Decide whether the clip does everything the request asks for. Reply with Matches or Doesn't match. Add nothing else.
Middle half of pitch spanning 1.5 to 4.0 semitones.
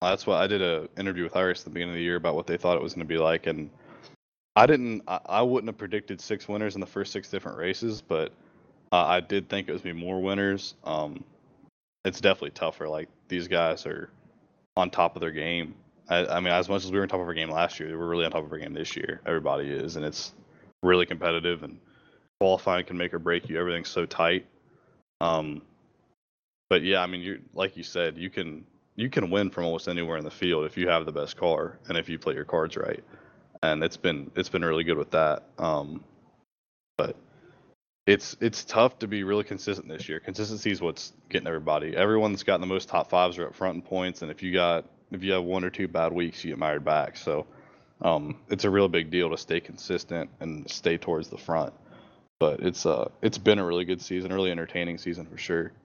Matches